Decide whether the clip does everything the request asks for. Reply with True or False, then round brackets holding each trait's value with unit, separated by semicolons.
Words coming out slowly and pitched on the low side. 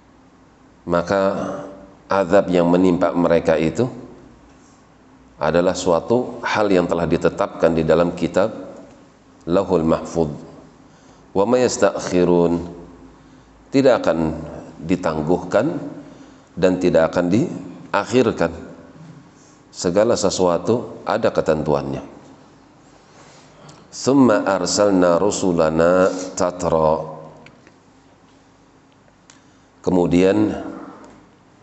True (65 wpm; 90 Hz)